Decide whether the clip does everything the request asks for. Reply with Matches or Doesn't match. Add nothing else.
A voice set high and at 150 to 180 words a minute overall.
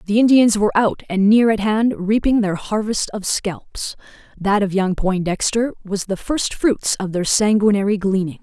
Matches